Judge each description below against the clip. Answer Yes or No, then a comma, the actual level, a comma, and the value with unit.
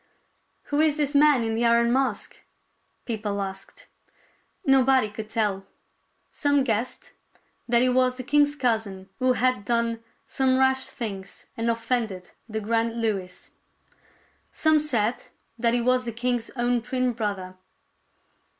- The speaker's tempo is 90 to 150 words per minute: Yes, average, 140 wpm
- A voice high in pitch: Yes, high, 235 Hz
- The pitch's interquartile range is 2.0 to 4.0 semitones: Yes, average, 2.9 semitones